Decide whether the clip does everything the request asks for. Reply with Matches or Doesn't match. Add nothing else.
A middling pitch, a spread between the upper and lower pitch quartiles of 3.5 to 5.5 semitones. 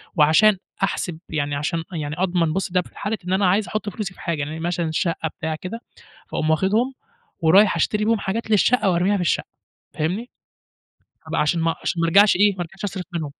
Matches